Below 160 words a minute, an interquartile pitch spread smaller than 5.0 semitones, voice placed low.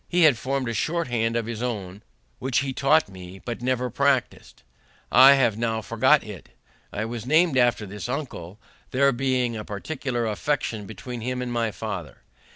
No: average, 180 wpm; average, 3.5 semitones; low, 120 Hz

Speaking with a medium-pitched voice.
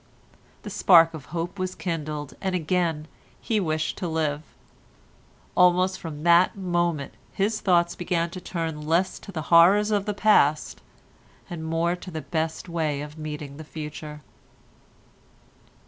Yes: medium, 170 Hz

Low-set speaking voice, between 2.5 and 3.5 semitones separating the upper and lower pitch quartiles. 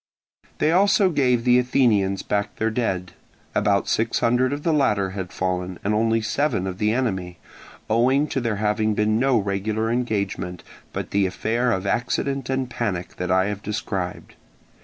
No: low, 110 Hz; average, 4.3 semitones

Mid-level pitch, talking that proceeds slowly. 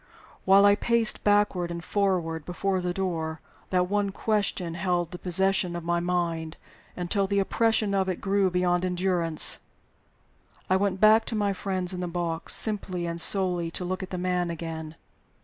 No: medium, 180 Hz; average, 165 wpm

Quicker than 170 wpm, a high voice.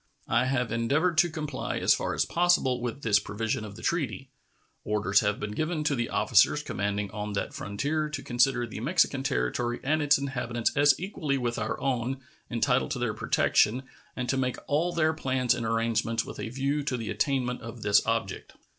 No: average, 190 wpm; low, 125 Hz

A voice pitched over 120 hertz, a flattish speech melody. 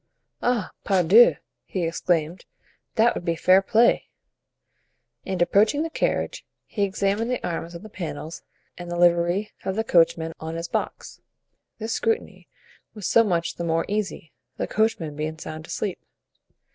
No: medium, 185 Hz; average, 4.3 semitones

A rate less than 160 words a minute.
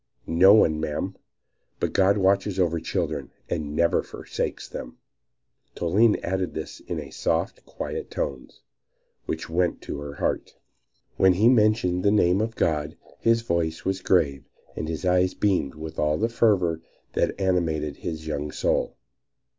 Yes: average, 145 wpm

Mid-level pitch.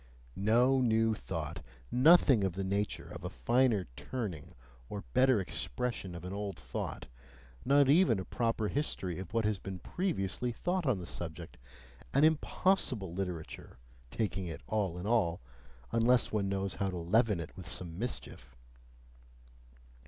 No: low, 100 Hz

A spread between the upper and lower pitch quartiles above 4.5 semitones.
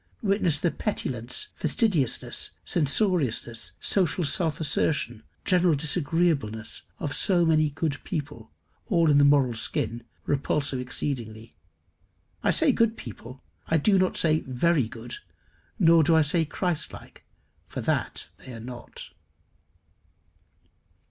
Yes: average, 5.1 semitones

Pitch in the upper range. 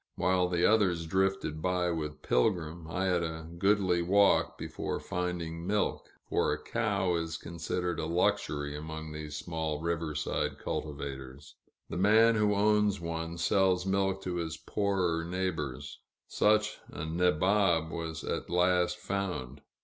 No: very low, 85 Hz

